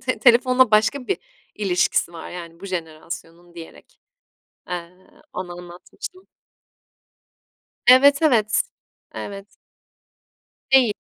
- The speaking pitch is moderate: No, high, 195 Hz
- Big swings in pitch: Yes, wide, 6.5 semitones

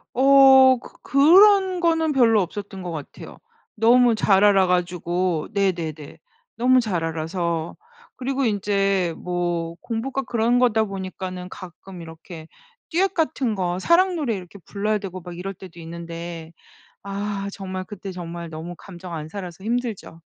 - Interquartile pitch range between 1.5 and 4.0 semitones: No, wide, 5.5 semitones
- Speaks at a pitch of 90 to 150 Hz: No, high, 195 Hz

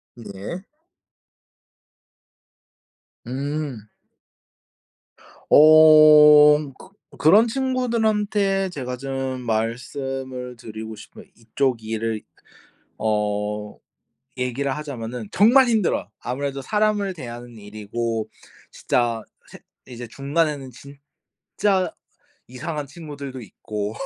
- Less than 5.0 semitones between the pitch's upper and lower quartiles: No, wide, 5.4 semitones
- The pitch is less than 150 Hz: Yes, low, 135 Hz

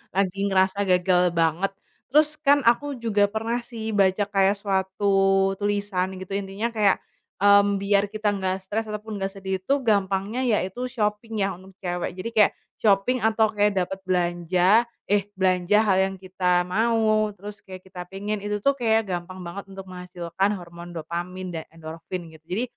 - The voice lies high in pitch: Yes, high, 195 Hz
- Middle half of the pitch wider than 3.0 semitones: No, narrow, 2.4 semitones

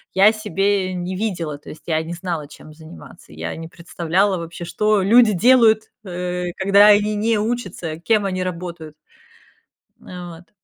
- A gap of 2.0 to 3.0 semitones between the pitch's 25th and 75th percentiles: No, average, 3.6 semitones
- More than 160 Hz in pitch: Yes, medium, 185 Hz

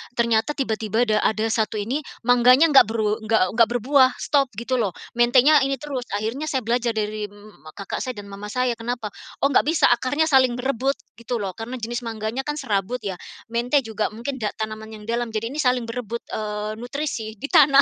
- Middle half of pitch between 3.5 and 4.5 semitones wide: No, average, 3.1 semitones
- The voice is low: No, high, 235 Hz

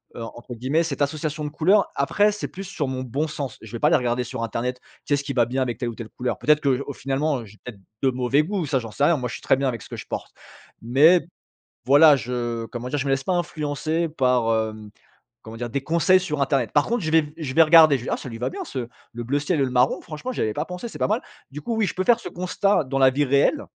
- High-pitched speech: No, medium, 140 Hz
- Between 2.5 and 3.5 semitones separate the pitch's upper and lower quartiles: No, average, 4.2 semitones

